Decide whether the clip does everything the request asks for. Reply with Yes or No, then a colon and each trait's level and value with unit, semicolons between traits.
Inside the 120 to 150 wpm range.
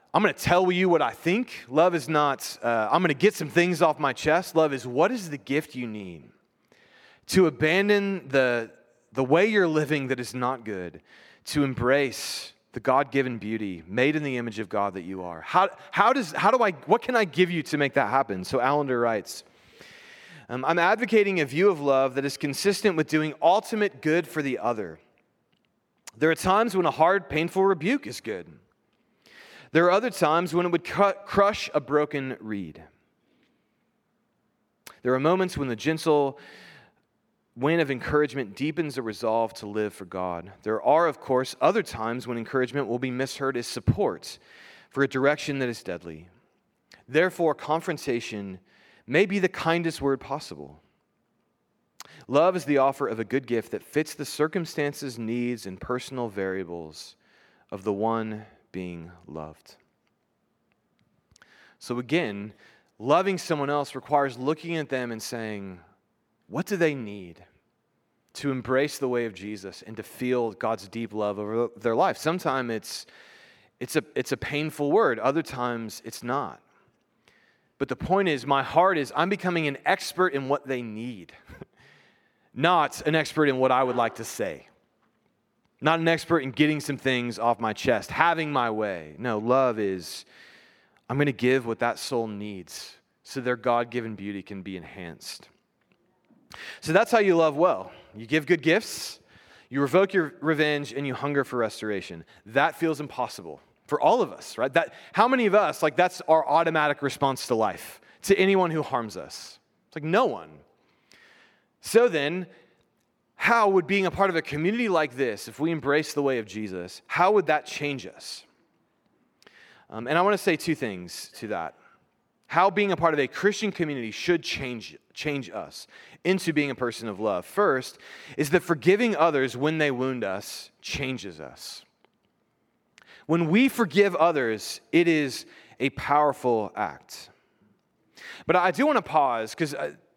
No: average, 170 wpm